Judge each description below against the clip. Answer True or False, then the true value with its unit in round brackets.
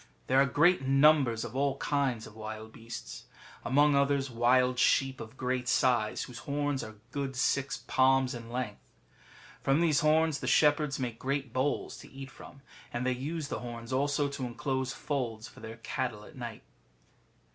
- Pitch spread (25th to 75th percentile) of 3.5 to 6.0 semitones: False (2.9 semitones)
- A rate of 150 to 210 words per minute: True (170 wpm)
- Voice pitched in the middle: False (130 Hz)